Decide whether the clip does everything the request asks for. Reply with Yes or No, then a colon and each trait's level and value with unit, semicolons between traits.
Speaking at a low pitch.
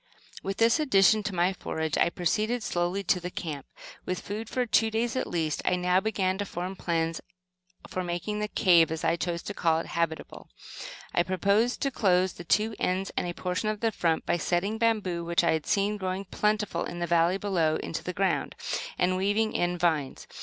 No: medium, 185 Hz